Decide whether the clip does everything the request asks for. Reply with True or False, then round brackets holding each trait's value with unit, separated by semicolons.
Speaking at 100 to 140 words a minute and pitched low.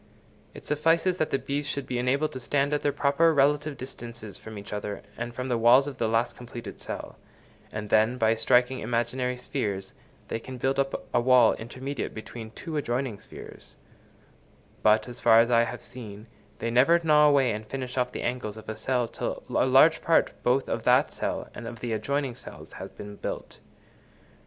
False (195 wpm; 125 Hz)